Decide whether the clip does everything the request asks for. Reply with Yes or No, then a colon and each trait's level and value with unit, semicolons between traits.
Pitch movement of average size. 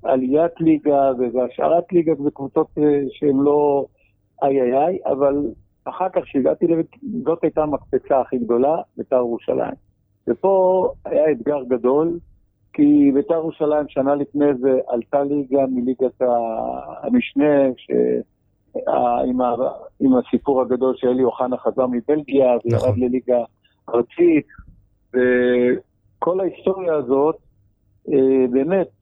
Yes: average, 3.5 semitones